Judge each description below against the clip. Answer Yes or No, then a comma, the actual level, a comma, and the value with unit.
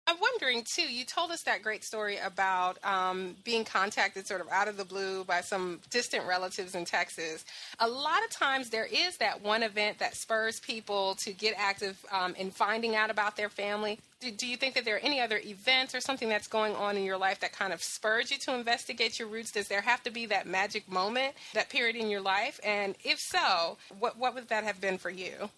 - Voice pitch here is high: Yes, high, 210 Hz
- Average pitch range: Yes, average, 3.9 semitones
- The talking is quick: Yes, fast, 230 wpm